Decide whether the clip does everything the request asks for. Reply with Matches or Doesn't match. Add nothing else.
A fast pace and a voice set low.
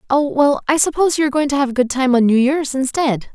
Doesn't match